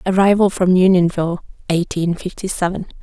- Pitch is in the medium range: Yes, medium, 180 Hz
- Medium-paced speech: No, slow, 120 wpm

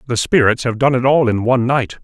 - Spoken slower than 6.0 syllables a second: No, 6.1 syllables/s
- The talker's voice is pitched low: Yes, low, 125 Hz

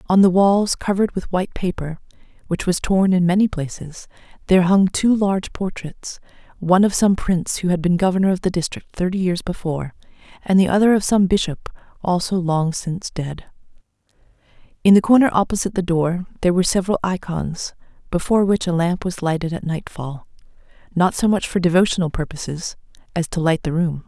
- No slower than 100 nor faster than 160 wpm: No, average, 175 wpm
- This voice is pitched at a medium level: Yes, medium, 180 Hz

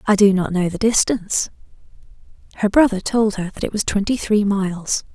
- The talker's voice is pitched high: Yes, high, 205 Hz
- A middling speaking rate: Yes, average, 185 wpm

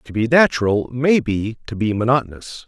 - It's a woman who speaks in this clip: No, male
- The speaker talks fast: No, average, 180 wpm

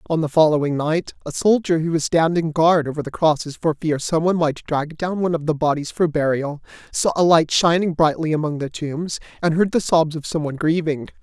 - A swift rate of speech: Yes, fast, 215 wpm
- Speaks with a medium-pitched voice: Yes, medium, 160 Hz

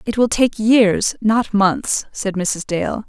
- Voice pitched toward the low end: No, high, 215 Hz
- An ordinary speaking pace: Yes, average, 155 wpm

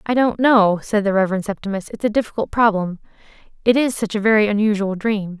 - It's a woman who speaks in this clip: Yes, female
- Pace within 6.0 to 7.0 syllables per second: Yes, 6.1 syllables/s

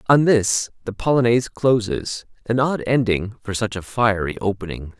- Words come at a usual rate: Yes, average, 155 wpm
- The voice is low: Yes, low, 110 Hz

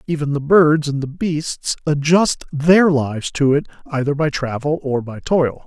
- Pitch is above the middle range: No, medium, 150 Hz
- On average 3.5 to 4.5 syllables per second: Yes, 4.3 syllables/s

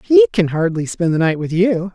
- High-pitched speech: No, medium, 170 Hz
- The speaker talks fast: Yes, fast, 245 wpm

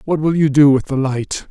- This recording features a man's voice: Yes, male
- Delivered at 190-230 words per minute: No, fast, 280 wpm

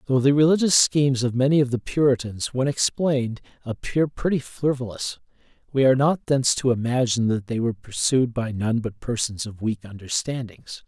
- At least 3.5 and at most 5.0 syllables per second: No, 5.5 syllables/s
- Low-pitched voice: Yes, low, 125 Hz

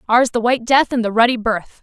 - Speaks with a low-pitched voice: No, high, 235 Hz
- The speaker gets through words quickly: Yes, fast, 265 wpm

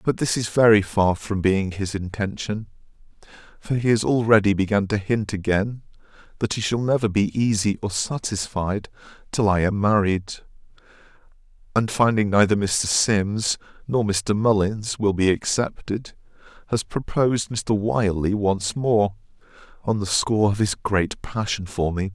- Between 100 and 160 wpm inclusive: Yes, average, 150 wpm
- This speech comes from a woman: No, male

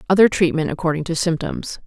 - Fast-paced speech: No, average, 160 wpm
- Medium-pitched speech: Yes, medium, 170 Hz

